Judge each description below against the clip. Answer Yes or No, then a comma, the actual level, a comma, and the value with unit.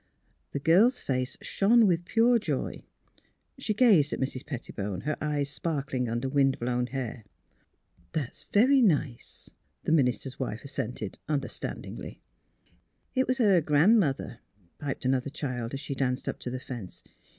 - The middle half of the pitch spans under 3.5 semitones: No, wide, 5.6 semitones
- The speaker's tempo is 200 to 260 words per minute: No, average, 160 wpm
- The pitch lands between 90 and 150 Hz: Yes, medium, 140 Hz